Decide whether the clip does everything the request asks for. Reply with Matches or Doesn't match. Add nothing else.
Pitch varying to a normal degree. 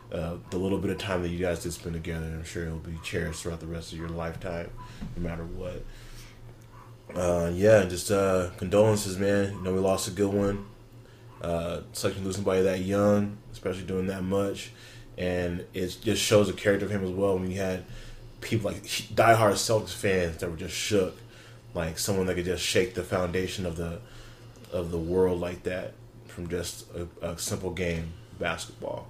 Matches